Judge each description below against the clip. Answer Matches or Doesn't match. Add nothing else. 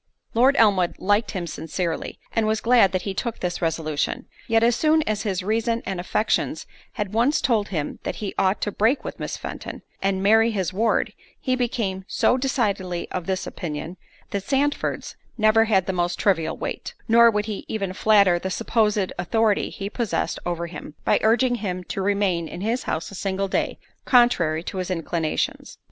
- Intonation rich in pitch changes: Doesn't match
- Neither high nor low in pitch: Doesn't match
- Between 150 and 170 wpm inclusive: Doesn't match